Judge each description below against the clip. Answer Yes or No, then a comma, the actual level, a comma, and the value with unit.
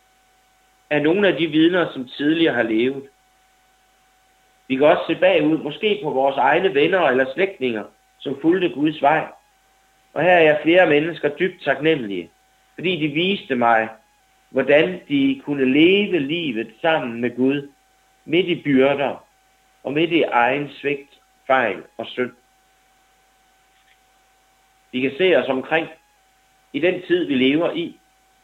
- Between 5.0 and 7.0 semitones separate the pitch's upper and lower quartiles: Yes, wide, 5.6 semitones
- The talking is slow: Yes, slow, 140 wpm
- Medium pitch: Yes, medium, 155 Hz